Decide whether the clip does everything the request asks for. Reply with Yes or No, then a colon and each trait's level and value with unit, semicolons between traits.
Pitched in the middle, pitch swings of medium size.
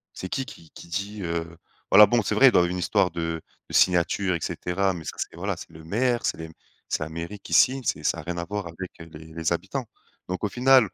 No: very low, 90 Hz; average, 3.8 semitones